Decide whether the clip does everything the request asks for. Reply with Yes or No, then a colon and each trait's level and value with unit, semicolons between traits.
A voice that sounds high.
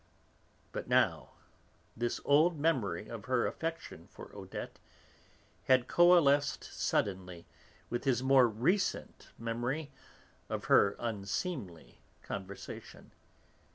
No: low, 120 Hz